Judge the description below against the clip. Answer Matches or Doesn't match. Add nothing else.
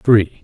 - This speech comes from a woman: Doesn't match